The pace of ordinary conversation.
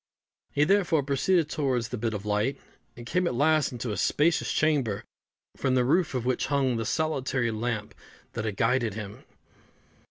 Yes: average, 170 wpm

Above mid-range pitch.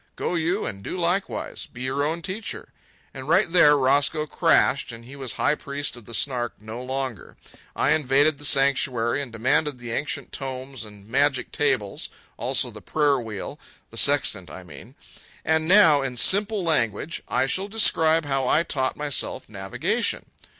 No: medium, 140 Hz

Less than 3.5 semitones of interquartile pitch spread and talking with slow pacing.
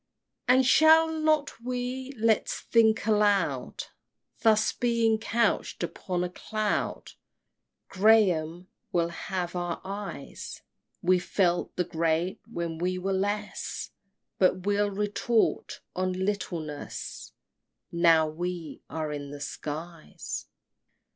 No: average, 4.4 semitones; slow, 110 wpm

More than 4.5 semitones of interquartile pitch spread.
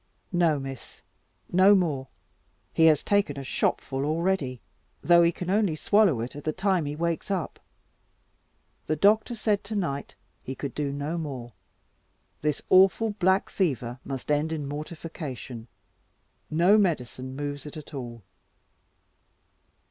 Yes: average, 5.2 semitones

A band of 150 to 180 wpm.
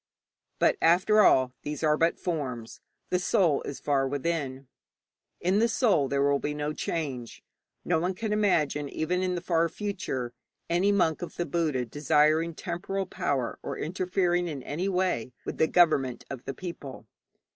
Yes: average, 165 wpm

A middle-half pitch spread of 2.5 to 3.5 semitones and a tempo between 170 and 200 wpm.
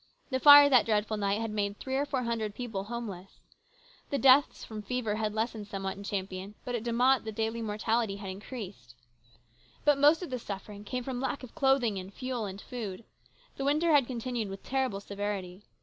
No: average, 4.1 semitones; average, 195 wpm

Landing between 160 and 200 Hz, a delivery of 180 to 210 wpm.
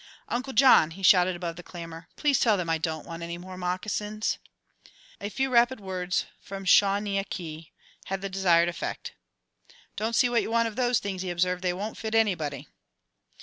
Yes: high, 190 Hz; average, 190 wpm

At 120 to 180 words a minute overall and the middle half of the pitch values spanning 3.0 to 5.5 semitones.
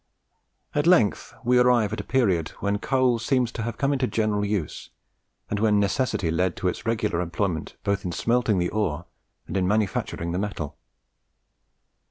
Yes: average, 170 wpm; average, 4.7 semitones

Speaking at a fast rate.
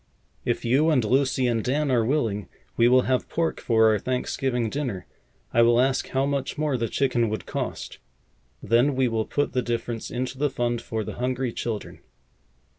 No: average, 185 wpm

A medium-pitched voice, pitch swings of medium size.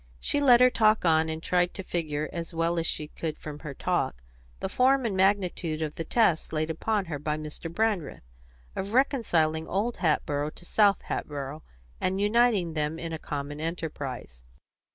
Yes: medium, 165 Hz; average, 4.8 semitones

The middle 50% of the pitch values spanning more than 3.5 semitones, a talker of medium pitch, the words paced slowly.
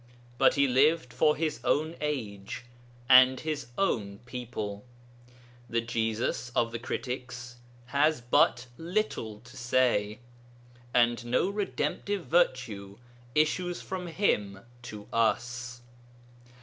No: average, 4.7 semitones; low, 125 Hz; slow, 110 wpm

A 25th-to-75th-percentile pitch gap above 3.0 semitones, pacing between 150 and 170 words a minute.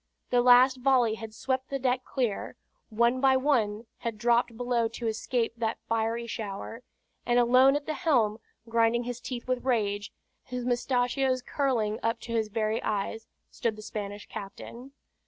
No: narrow, 2.4 semitones; average, 160 wpm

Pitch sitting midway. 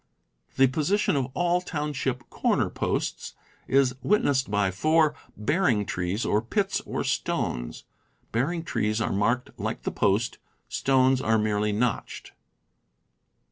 No: low, 125 Hz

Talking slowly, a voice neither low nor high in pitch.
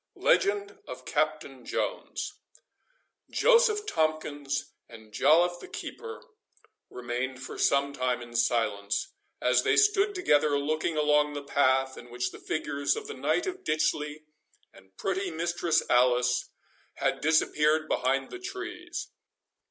Yes: slow, 130 wpm; medium, 150 Hz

